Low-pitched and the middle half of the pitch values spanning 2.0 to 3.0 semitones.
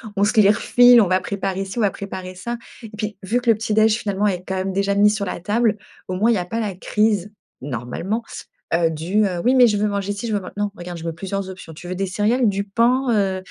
No: high, 200 Hz; narrow, 2.6 semitones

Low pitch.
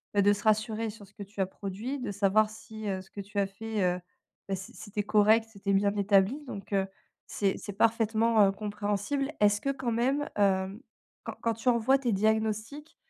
No: high, 210 Hz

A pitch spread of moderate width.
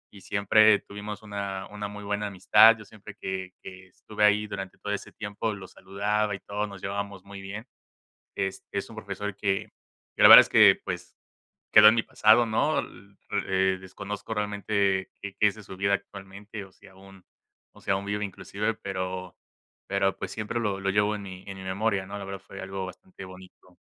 No: narrow, 1.4 semitones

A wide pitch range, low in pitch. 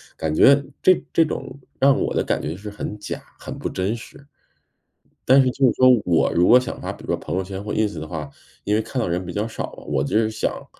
Yes: wide, 6.3 semitones; low, 105 Hz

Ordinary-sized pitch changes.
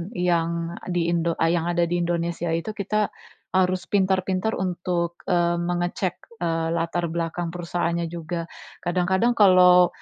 No: narrow, 1.4 semitones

